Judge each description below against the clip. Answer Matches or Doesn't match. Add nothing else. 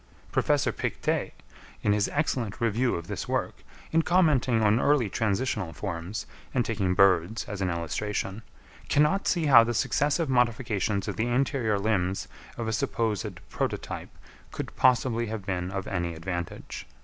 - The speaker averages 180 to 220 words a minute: Doesn't match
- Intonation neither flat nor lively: Matches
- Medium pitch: Doesn't match